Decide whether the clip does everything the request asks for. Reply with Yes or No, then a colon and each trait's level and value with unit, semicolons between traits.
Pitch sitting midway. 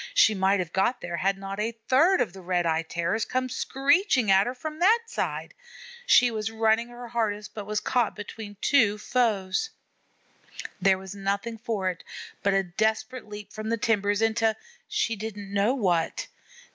No: high, 215 Hz